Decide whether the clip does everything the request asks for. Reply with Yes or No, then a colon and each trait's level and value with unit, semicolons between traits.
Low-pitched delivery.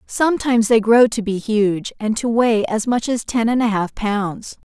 No: high, 225 Hz